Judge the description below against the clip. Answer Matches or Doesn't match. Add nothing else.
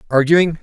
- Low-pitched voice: Doesn't match